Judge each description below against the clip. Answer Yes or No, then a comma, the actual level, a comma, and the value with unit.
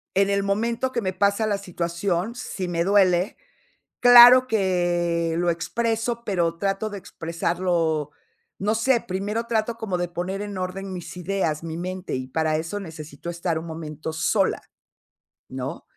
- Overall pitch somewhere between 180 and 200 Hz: Yes, medium, 185 Hz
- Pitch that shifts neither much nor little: Yes, average, 3.6 semitones